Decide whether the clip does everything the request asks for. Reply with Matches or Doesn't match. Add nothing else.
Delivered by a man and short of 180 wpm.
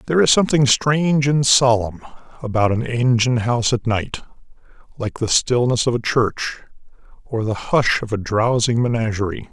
Matches